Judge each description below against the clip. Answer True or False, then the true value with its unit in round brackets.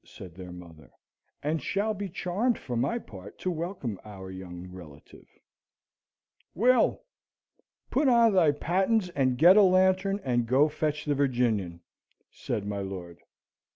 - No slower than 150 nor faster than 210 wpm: False (140 wpm)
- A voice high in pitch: False (145 Hz)